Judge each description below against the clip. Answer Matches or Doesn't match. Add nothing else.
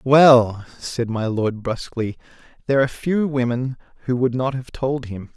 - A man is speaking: Matches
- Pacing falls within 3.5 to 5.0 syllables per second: Matches